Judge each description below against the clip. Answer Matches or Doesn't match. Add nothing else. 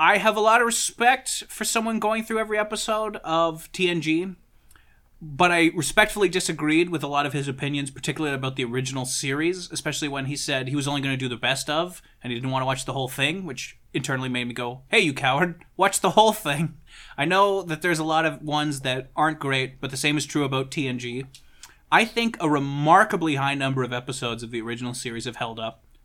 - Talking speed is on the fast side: Matches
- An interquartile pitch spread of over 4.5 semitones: Matches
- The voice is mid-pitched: Matches